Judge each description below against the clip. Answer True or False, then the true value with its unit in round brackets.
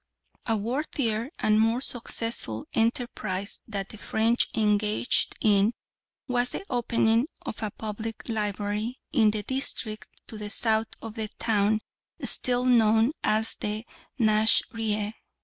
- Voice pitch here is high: True (220 Hz)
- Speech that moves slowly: True (125 wpm)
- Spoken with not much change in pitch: True (1.7 semitones)